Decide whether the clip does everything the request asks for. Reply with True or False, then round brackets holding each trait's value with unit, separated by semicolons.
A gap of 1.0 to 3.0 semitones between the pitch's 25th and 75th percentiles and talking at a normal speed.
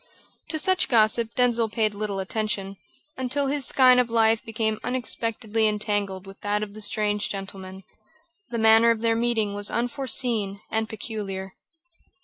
True (2.4 semitones; 145 wpm)